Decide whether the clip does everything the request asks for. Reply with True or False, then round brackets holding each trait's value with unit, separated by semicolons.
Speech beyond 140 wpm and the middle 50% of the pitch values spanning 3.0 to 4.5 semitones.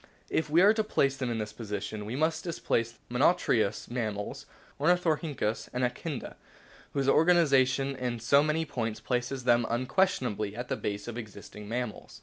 False (170 wpm; 5.2 semitones)